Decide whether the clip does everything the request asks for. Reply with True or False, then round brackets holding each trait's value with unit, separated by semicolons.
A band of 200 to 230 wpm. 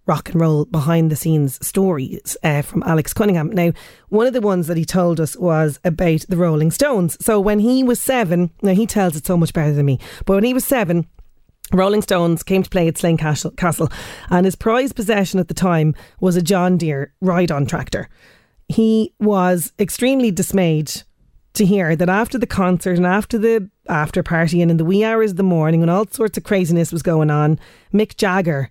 True (205 wpm)